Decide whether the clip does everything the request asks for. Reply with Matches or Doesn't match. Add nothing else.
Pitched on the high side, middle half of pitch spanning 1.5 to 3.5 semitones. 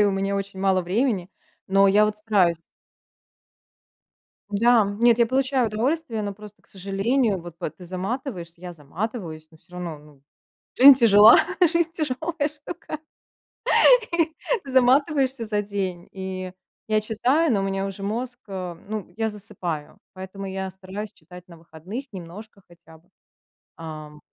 Doesn't match